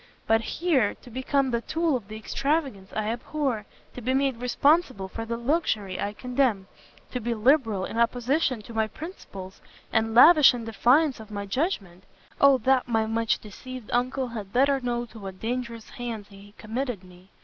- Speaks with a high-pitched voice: Yes, high, 235 Hz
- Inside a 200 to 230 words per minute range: No, average, 175 wpm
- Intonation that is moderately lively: Yes, average, 3.8 semitones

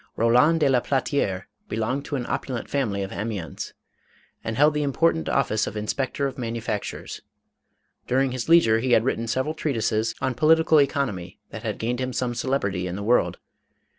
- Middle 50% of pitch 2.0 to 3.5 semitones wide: No, average, 4.0 semitones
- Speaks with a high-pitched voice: No, low, 125 Hz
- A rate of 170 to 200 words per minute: Yes, average, 175 wpm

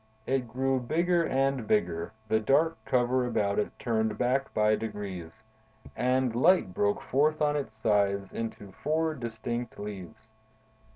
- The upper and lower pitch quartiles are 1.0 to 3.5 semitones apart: No, average, 4.3 semitones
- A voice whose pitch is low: Yes, low, 120 Hz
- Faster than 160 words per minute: No, slow, 135 wpm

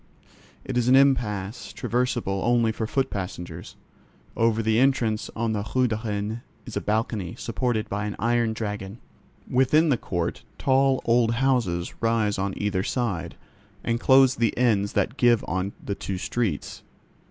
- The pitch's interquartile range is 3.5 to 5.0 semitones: No, average, 3.1 semitones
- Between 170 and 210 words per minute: No, average, 155 wpm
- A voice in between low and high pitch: No, low, 115 Hz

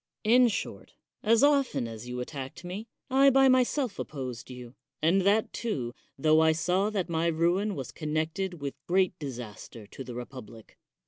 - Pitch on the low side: No, medium, 165 Hz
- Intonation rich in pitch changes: Yes, wide, 8.3 semitones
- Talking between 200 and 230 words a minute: No, average, 165 wpm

